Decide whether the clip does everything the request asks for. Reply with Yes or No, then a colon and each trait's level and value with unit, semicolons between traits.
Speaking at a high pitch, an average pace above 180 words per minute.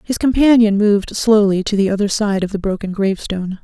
Yes: high, 205 Hz; average, 200 wpm